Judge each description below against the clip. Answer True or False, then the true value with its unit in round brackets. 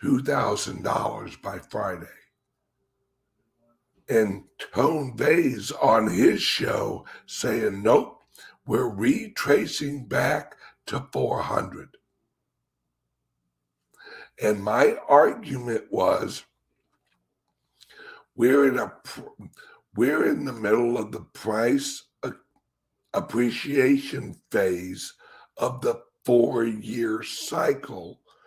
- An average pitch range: False (6.0 semitones)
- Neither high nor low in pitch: False (120 Hz)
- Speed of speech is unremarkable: False (80 wpm)